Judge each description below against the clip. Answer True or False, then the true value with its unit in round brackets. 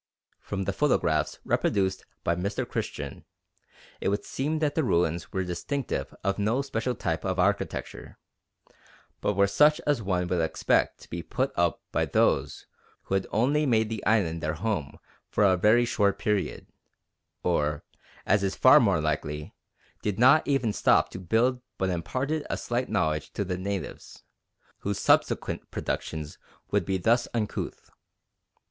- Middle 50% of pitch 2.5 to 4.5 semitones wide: False (5.2 semitones)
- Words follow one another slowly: False (155 wpm)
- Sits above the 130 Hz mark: False (100 Hz)